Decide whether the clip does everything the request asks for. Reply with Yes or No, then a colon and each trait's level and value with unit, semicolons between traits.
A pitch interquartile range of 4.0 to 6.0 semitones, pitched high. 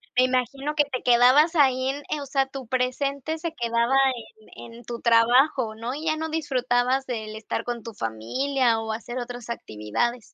No: average, 2.9 semitones; very high, 250 Hz